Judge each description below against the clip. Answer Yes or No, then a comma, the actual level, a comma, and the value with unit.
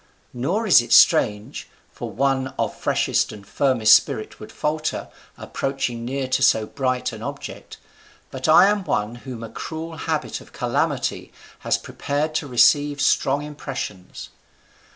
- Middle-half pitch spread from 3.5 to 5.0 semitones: Yes, average, 4.1 semitones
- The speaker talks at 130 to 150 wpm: Yes, average, 145 wpm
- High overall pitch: No, low, 135 Hz